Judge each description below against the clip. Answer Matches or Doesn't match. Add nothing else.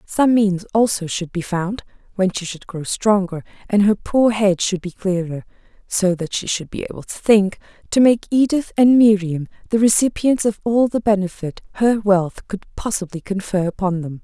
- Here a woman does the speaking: Matches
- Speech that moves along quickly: Doesn't match